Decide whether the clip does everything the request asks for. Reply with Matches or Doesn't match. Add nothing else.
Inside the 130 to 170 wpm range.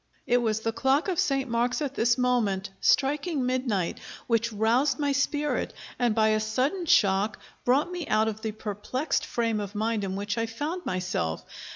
Doesn't match